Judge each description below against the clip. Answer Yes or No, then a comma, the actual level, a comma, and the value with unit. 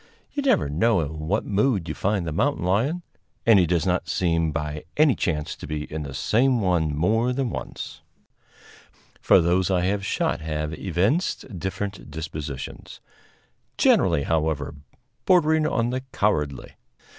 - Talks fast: No, average, 150 wpm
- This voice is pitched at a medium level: No, very low, 90 Hz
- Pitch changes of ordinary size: No, wide, 6.7 semitones